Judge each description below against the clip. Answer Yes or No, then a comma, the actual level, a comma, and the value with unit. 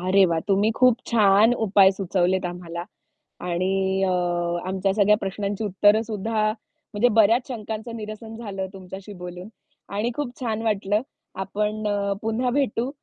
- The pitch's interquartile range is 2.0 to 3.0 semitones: Yes, narrow, 2.5 semitones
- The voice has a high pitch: Yes, high, 205 Hz